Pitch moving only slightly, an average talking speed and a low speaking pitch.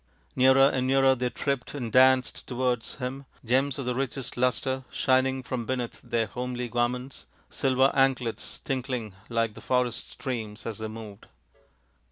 Yes: narrow, 2.0 semitones; average, 155 wpm; low, 125 Hz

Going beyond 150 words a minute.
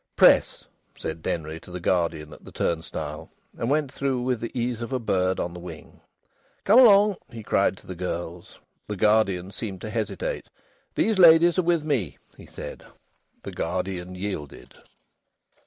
Yes: average, 165 wpm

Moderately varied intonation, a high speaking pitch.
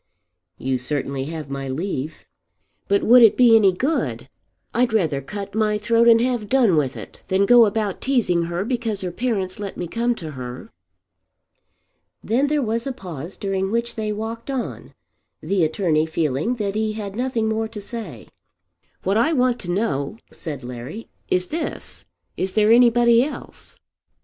No: wide, 5.7 semitones; high, 210 Hz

